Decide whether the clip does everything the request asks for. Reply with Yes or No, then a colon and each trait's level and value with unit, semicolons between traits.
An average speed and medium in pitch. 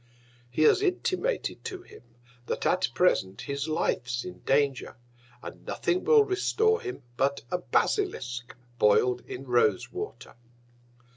No: slow, 130 wpm; medium, 155 Hz